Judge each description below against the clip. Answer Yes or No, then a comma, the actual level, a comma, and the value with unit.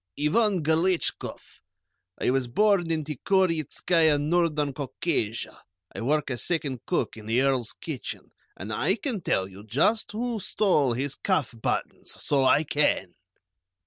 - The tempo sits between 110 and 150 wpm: Yes, average, 140 wpm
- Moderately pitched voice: Yes, medium, 150 Hz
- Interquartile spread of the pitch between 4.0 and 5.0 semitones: No, wide, 5.6 semitones